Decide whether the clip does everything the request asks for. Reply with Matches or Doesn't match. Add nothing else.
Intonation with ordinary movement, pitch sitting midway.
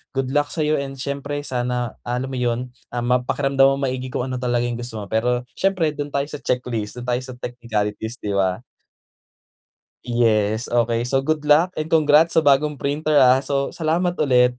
Doesn't match